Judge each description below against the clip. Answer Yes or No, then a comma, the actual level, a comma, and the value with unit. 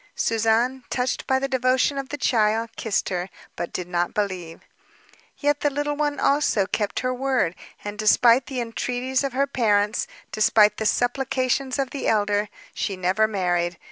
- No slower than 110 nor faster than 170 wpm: Yes, average, 165 wpm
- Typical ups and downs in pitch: Yes, average, 4.3 semitones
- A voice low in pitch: No, high, 230 Hz